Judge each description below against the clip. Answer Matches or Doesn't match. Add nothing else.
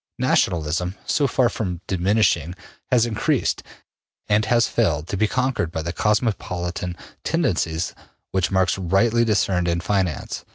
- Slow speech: Matches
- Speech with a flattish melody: Doesn't match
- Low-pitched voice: Matches